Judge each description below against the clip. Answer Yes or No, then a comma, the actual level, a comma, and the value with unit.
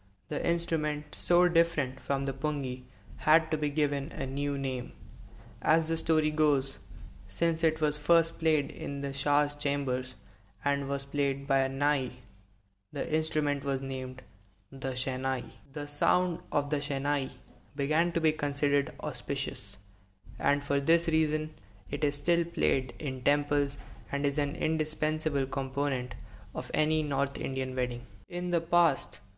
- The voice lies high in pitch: No, medium, 140 Hz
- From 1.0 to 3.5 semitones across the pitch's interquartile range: Yes, average, 2.8 semitones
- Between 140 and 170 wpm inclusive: Yes, average, 145 wpm